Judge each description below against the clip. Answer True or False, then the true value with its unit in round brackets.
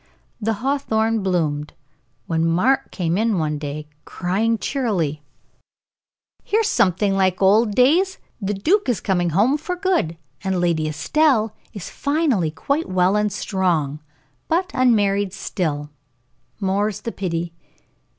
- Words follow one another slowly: True (125 wpm)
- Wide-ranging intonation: True (6.0 semitones)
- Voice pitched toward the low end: False (195 Hz)